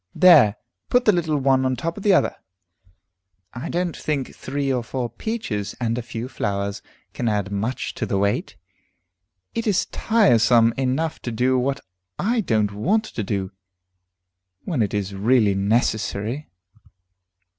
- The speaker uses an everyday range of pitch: No, wide, 6.9 semitones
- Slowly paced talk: No, average, 155 wpm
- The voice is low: Yes, low, 125 Hz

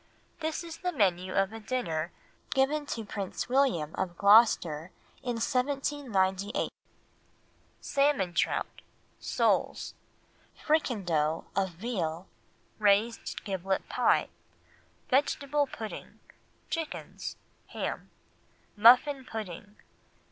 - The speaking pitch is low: No, high, 215 Hz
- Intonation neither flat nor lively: No, wide, 6.3 semitones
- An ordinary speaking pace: No, slow, 90 wpm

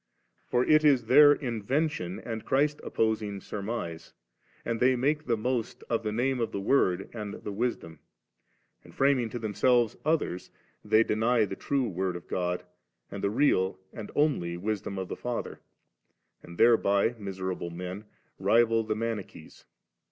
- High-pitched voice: No, low, 110 Hz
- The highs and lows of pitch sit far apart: No, average, 4.2 semitones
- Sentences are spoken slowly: No, average, 160 wpm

